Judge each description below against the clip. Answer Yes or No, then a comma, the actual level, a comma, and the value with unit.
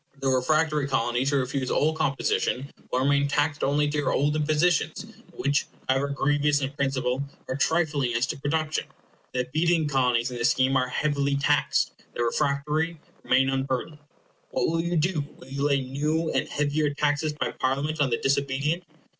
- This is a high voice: No, medium, 140 Hz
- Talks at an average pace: Yes, average, 170 wpm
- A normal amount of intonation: No, narrow, 2.3 semitones